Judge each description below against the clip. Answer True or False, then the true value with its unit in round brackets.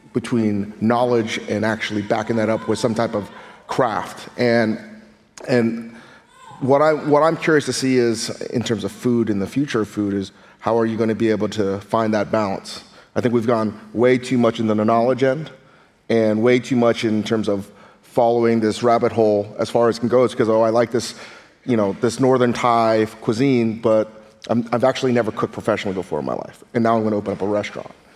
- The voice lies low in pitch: True (115 Hz)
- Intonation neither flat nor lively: False (2.0 semitones)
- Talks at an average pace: False (215 wpm)